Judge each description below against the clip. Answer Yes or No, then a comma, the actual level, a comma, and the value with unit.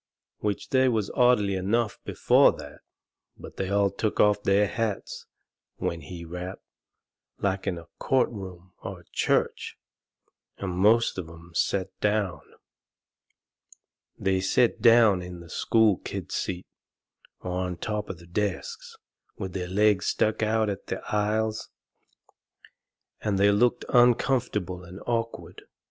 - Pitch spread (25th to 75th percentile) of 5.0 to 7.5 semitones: No, average, 3.2 semitones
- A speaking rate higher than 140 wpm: No, slow, 135 wpm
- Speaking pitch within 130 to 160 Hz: No, low, 100 Hz